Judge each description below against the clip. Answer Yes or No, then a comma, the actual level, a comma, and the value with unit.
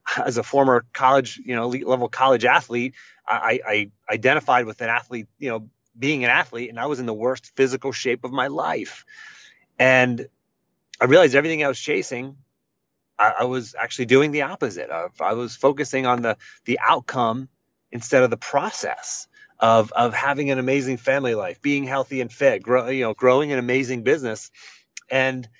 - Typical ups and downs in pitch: No, narrow, 2.2 semitones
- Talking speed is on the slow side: No, average, 180 wpm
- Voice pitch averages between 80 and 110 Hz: No, low, 125 Hz